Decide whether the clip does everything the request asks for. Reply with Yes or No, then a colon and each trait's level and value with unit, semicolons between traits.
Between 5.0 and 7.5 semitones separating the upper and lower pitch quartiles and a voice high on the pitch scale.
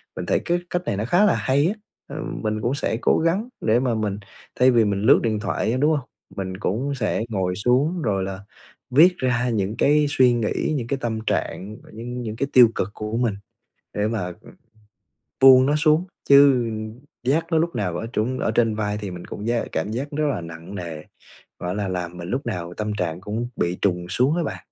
No: wide, 5.4 semitones; low, 115 Hz